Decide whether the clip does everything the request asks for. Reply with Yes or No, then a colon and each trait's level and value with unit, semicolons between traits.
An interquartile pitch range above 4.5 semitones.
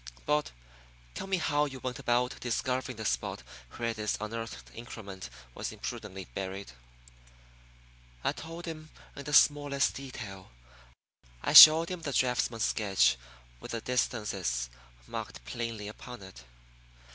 Yes: wide, 5.5 semitones